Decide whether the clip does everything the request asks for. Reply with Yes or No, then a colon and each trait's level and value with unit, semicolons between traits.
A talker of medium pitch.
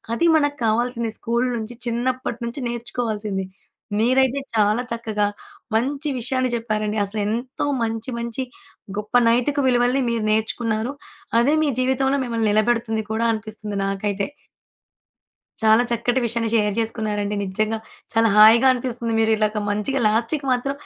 No: high, 230 Hz